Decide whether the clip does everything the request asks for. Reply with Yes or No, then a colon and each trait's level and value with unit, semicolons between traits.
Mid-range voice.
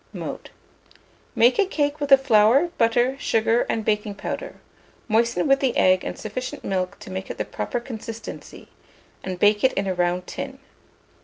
No: high, 230 Hz